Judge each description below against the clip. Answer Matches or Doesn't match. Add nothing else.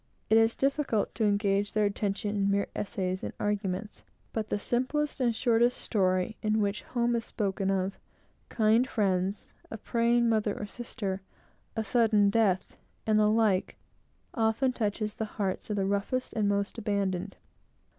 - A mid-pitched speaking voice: Doesn't match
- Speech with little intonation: Matches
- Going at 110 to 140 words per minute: Doesn't match